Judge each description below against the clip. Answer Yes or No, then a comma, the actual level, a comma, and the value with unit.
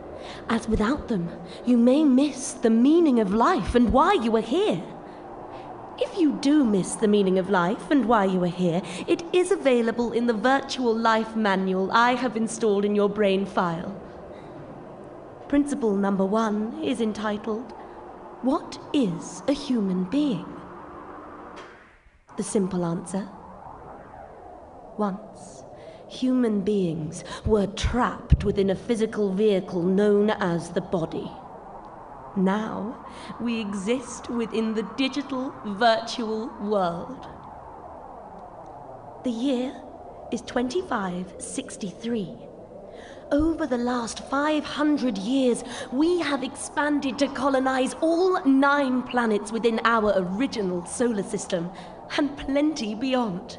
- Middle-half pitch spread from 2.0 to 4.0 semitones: No, average, 4.9 semitones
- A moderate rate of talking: No, slow, 115 wpm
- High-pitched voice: Yes, high, 230 Hz